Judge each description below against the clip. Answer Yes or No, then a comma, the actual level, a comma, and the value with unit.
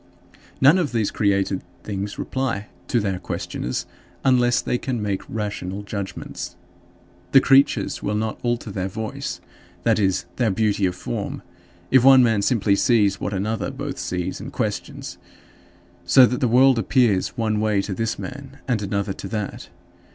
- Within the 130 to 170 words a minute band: Yes, average, 160 wpm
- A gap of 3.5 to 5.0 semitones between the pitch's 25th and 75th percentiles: Yes, average, 3.8 semitones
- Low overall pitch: Yes, low, 110 Hz